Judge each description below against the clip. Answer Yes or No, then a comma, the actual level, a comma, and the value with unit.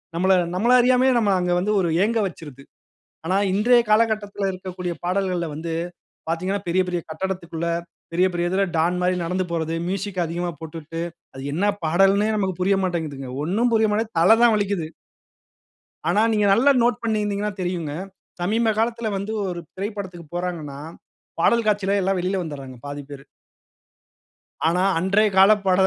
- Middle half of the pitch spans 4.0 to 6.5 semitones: No, average, 3.5 semitones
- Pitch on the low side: No, medium, 185 Hz